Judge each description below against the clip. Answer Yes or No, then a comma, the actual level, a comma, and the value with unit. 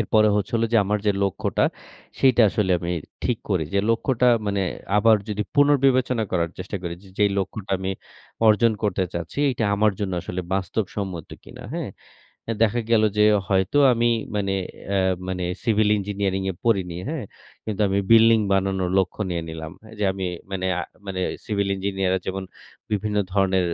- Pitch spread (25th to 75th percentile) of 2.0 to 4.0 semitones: Yes, average, 2.8 semitones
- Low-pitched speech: Yes, low, 100 Hz